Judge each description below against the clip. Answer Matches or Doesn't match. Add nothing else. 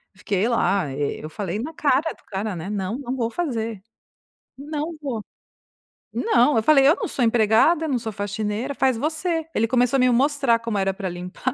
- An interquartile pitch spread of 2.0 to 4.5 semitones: Doesn't match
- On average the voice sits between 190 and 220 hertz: Doesn't match